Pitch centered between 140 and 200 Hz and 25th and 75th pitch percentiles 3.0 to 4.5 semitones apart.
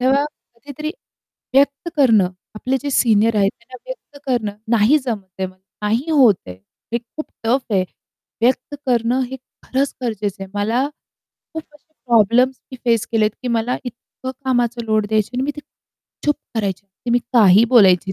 No: high, 235 Hz; average, 3.9 semitones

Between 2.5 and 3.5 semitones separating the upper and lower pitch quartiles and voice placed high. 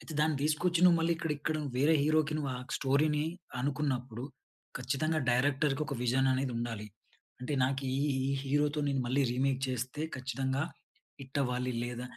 No: average, 2.9 semitones; low, 135 Hz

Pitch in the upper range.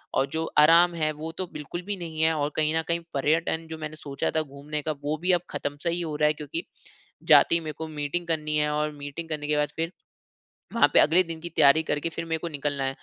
No: medium, 155 Hz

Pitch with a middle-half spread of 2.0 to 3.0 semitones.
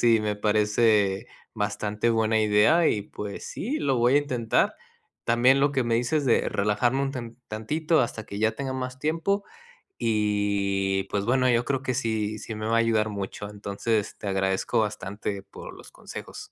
No: average, 3.6 semitones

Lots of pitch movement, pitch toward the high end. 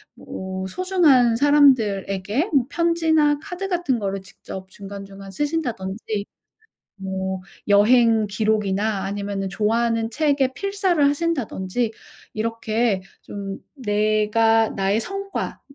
Yes: wide, 6.5 semitones; high, 225 Hz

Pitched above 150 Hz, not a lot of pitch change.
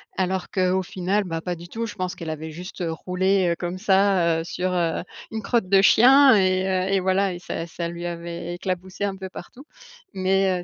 Yes: medium, 185 Hz; narrow, 1.9 semitones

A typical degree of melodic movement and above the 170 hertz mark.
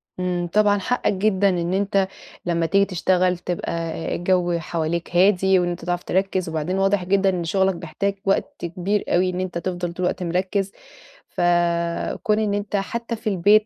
No: narrow, 2.2 semitones; medium, 185 Hz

